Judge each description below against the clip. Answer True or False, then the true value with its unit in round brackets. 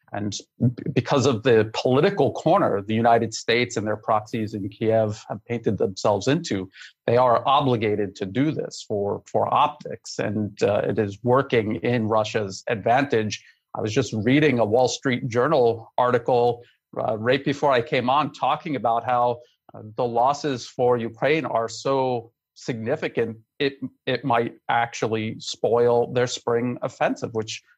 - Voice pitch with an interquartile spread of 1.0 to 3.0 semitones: True (2.5 semitones)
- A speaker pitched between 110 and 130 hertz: True (120 Hz)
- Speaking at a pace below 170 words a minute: True (150 wpm)